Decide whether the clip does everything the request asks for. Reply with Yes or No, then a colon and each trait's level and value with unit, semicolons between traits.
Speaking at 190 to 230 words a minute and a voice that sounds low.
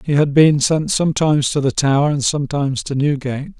No: average, 200 wpm; medium, 145 Hz